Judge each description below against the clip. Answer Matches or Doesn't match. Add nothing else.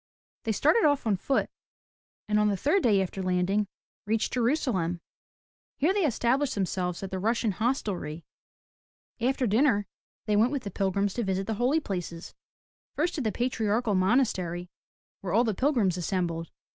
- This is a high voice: Matches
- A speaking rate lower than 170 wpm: Matches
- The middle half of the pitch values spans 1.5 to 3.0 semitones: Doesn't match